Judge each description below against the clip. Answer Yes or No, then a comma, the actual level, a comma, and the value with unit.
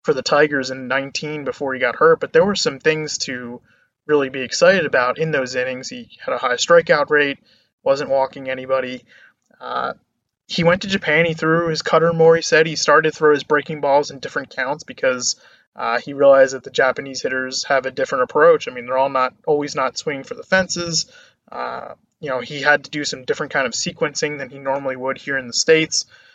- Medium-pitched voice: Yes, medium, 145 Hz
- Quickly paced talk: Yes, fast, 220 wpm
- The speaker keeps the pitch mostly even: No, average, 3.4 semitones